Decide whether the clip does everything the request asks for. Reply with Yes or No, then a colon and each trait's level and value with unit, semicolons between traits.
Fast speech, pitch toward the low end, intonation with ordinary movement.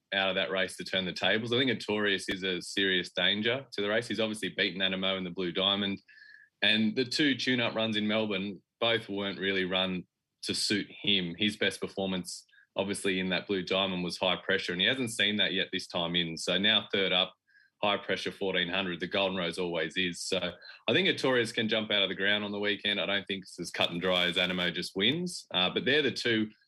No: fast, 230 wpm; very low, 95 Hz; narrow, 2.1 semitones